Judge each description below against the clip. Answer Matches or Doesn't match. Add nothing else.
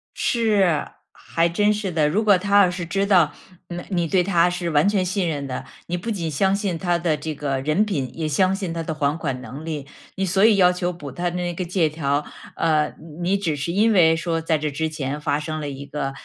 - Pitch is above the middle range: Doesn't match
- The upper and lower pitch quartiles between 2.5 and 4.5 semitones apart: Matches